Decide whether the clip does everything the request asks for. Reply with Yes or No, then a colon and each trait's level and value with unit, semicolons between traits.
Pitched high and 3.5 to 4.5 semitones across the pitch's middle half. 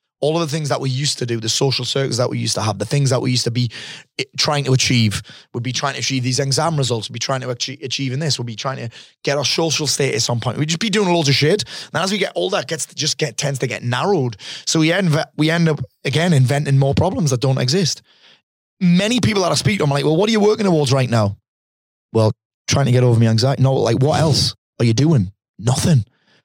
No: low, 135 Hz; average, 4.0 semitones